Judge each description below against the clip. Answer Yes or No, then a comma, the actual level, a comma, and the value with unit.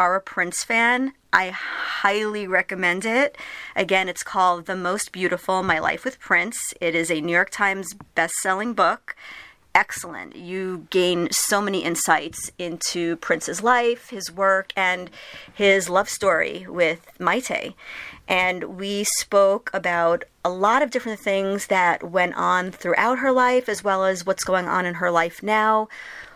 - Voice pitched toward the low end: No, high, 190 Hz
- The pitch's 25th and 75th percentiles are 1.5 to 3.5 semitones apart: Yes, average, 2.9 semitones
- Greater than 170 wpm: No, average, 155 wpm